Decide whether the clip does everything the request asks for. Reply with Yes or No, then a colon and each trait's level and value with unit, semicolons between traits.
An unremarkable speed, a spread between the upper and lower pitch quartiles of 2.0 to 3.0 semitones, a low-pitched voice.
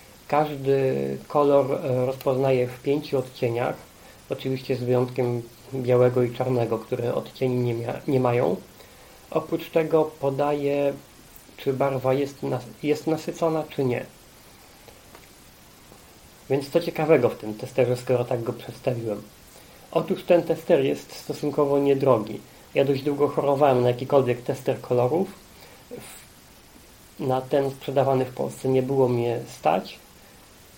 Yes: average, 120 wpm; narrow, 2.5 semitones; low, 130 Hz